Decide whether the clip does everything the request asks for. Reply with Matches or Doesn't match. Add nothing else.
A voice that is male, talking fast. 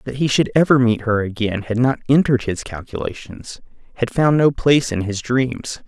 Doesn't match